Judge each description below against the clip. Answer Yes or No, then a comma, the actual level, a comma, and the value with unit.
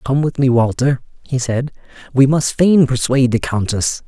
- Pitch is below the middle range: Yes, low, 130 Hz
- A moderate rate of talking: Yes, average, 175 wpm